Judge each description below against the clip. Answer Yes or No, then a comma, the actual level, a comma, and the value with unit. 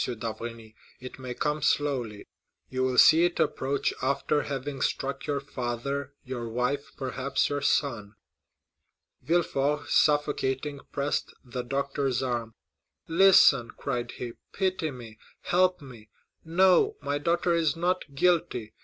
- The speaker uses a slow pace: Yes, slow, 125 wpm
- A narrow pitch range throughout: No, average, 3.4 semitones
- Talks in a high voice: No, medium, 140 Hz